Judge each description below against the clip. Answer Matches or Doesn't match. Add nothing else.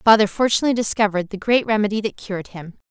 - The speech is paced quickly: Doesn't match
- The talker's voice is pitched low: Doesn't match